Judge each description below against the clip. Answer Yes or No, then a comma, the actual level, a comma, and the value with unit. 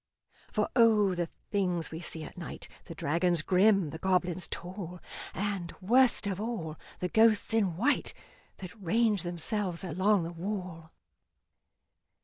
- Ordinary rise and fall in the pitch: Yes, average, 3.5 semitones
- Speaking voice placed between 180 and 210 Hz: Yes, medium, 185 Hz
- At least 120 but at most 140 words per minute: Yes, slow, 135 wpm